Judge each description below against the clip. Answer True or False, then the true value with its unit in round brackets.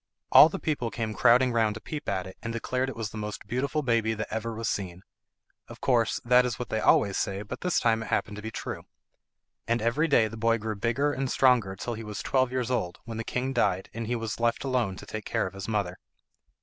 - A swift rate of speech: True (245 wpm)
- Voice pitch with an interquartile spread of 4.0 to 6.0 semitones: False (2.8 semitones)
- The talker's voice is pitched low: True (115 Hz)